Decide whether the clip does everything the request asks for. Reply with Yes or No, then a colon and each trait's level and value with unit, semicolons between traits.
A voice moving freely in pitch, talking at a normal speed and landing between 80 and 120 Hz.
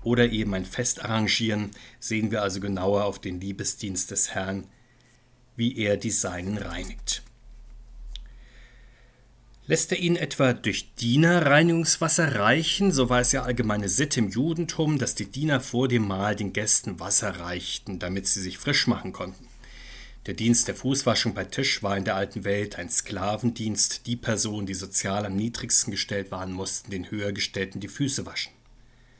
No: average, 4.0 semitones; average, 160 wpm; low, 110 Hz